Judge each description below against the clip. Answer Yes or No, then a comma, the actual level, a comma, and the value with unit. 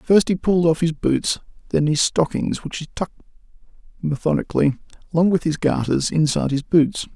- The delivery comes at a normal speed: Yes, average, 170 wpm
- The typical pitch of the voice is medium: Yes, medium, 160 Hz